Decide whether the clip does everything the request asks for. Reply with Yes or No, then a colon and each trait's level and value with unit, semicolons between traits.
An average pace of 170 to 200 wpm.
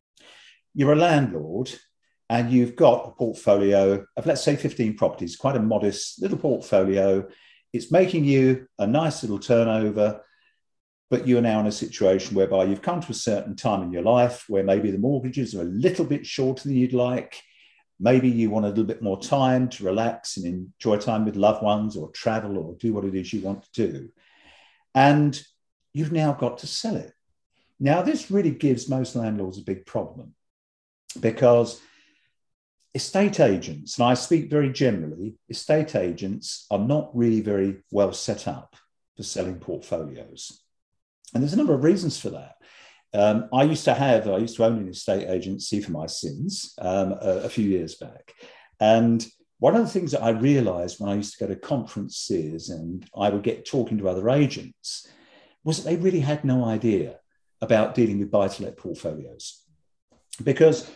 Yes: average, 180 wpm